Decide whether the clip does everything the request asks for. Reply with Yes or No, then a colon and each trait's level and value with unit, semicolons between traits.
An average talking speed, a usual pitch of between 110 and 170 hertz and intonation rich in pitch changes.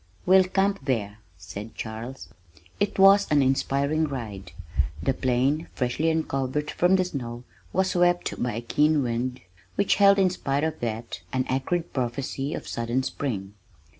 Yes: average, 150 wpm; low, 135 Hz; wide, 6.2 semitones